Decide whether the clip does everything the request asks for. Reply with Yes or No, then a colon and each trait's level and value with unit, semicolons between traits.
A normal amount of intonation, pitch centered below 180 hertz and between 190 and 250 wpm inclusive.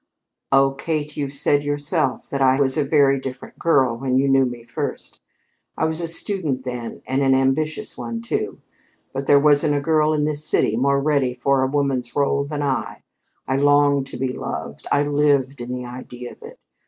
No: narrow, 1.8 semitones; medium, 140 Hz; average, 195 wpm